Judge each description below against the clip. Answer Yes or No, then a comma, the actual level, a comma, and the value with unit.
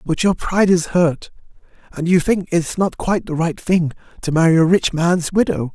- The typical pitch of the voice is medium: Yes, medium, 170 Hz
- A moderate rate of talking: No, fast, 210 wpm